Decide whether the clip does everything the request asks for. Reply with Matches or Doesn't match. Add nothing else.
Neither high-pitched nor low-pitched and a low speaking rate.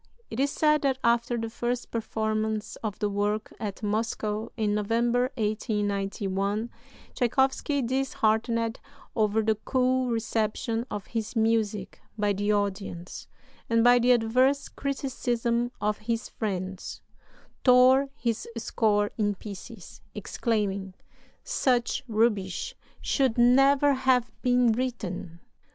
Doesn't match